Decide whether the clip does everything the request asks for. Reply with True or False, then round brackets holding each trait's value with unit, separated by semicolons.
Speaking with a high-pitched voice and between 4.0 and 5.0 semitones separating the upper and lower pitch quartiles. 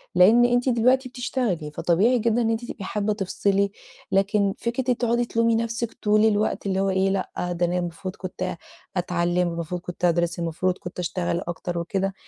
True (195 Hz; 4.5 semitones)